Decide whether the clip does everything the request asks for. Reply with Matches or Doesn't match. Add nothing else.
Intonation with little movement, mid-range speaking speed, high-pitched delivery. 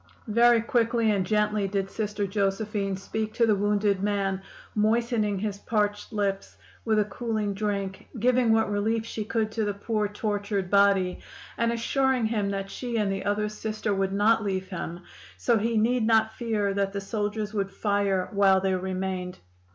Matches